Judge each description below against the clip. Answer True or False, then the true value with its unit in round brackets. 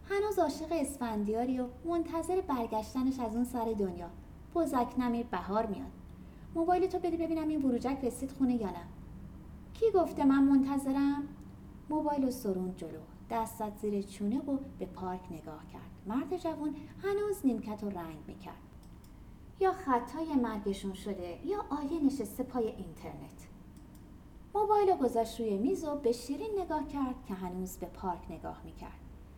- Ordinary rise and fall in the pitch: False (6.4 semitones)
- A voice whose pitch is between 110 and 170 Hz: False (255 Hz)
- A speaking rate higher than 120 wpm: True (145 wpm)